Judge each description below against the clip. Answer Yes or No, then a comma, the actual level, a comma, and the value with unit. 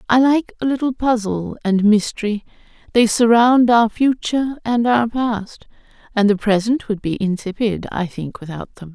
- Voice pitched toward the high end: Yes, high, 225 Hz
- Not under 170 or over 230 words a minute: No, average, 155 wpm